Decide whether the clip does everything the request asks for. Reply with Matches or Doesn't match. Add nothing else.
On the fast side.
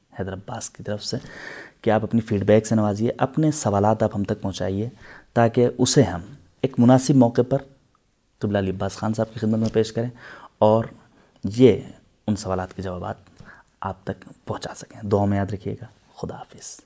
Doesn't match